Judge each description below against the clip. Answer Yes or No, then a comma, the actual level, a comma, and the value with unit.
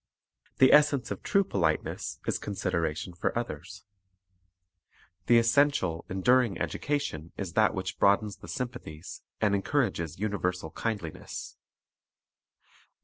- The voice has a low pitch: Yes, low, 100 Hz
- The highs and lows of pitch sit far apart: Yes, wide, 6.0 semitones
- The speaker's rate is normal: No, slow, 110 wpm